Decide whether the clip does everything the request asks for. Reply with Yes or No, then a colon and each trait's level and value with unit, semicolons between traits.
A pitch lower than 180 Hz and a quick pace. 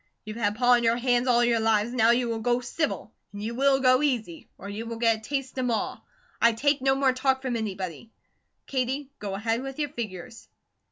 No: high, 240 Hz; fast, 220 wpm